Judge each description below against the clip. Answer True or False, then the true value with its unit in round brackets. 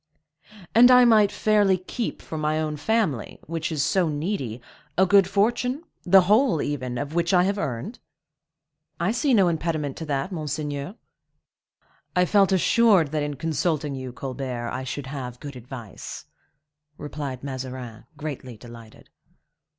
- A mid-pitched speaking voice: True (155 Hz)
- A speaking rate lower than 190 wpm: True (145 wpm)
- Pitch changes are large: True (6.3 semitones)